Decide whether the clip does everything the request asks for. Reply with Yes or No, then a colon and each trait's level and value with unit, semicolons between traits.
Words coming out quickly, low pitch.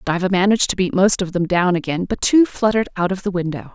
No: fast, 255 wpm; medium, 185 Hz